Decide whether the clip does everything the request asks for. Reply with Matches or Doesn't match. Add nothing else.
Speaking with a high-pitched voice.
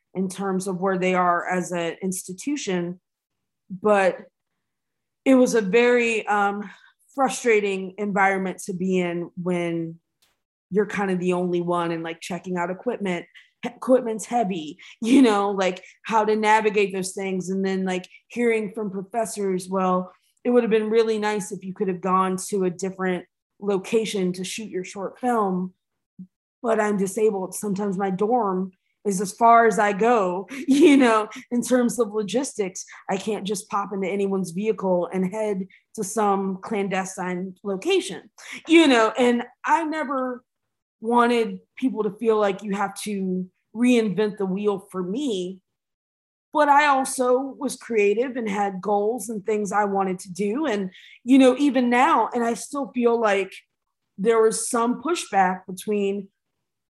Matches